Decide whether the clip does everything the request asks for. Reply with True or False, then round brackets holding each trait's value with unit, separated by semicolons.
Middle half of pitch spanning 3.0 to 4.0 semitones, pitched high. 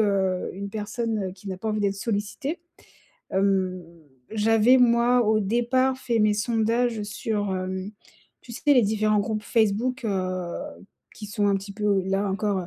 False (2.6 semitones; 210 Hz)